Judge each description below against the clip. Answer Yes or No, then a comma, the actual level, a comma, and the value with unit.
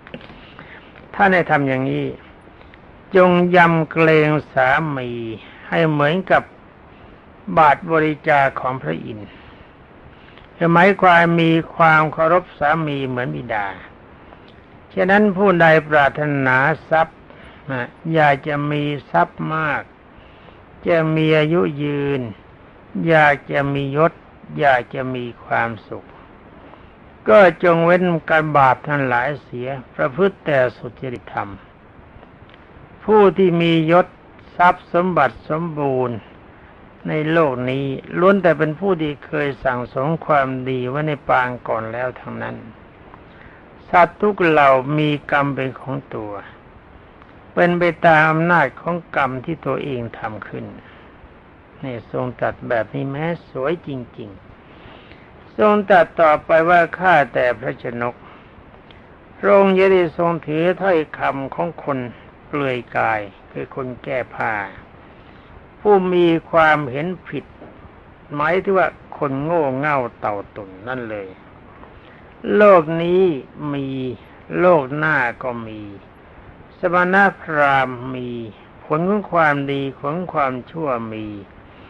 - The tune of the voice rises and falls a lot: No, average, 4.8 semitones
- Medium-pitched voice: Yes, medium, 150 Hz